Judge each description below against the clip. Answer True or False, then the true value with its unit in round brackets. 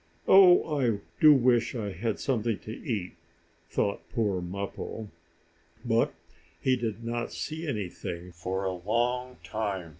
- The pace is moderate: False (130 wpm)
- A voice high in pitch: False (110 Hz)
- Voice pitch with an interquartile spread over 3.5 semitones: True (4.2 semitones)